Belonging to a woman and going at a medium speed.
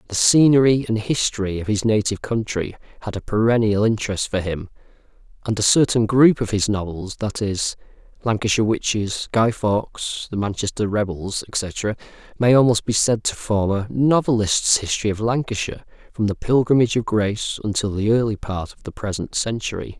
No: male; average, 160 wpm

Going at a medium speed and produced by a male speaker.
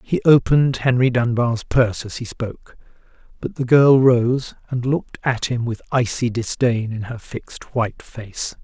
Yes: average, 165 wpm; male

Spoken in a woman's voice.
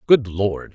No: male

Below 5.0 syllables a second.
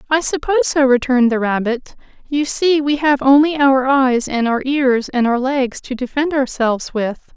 Yes: 4.7 syllables/s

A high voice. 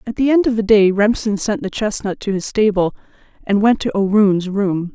Yes: high, 205 Hz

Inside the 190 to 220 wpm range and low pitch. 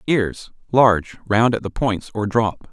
No: average, 155 wpm; low, 110 Hz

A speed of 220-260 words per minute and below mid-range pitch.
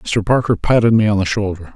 Yes: fast, 240 wpm; low, 105 Hz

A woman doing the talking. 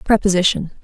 Yes: female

